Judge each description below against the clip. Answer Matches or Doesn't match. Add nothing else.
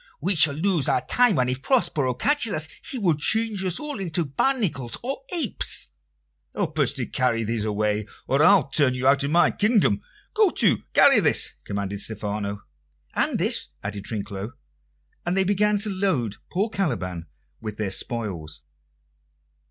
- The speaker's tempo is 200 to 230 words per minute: Doesn't match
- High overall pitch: Doesn't match